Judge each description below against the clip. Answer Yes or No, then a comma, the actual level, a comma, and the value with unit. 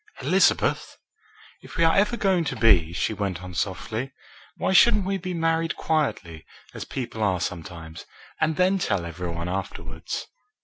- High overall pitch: No, low, 110 Hz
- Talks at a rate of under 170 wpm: Yes, average, 160 wpm